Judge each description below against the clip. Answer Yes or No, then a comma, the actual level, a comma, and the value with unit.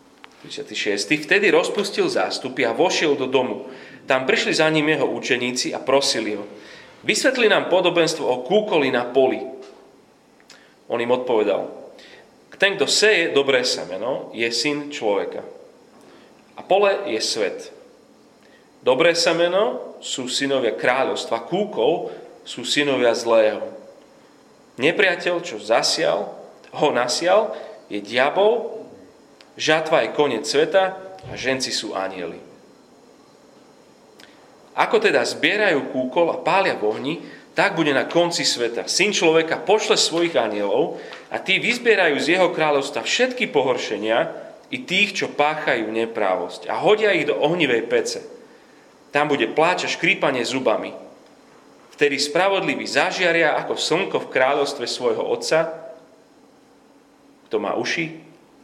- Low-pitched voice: No, medium, 165 Hz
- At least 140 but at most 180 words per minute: No, average, 120 wpm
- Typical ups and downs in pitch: No, wide, 8.0 semitones